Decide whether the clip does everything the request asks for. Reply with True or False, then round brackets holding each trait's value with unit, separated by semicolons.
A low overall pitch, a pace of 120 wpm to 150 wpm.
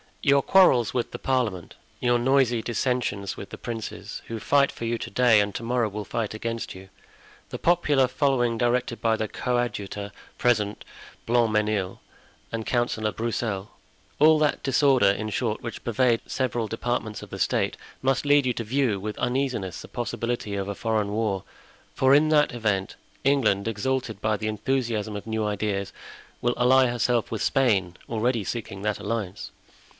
False (115 Hz; 165 wpm)